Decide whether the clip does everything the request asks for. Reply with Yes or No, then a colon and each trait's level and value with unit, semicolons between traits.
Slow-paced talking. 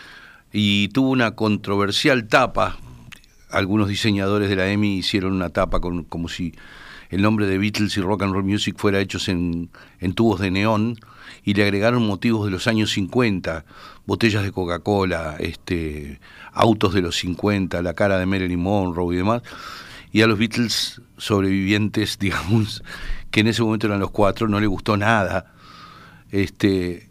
No: average, 160 wpm